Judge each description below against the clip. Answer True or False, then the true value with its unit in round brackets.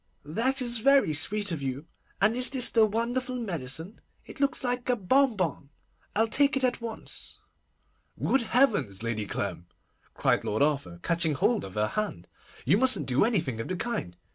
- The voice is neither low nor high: False (205 Hz)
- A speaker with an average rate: True (170 wpm)